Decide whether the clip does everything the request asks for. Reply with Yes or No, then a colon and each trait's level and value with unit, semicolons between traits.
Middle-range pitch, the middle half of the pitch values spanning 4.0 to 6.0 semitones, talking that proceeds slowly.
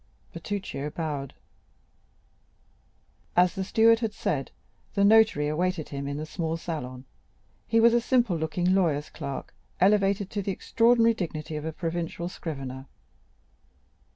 Yes: medium, 175 Hz; average, 5.2 semitones; slow, 130 wpm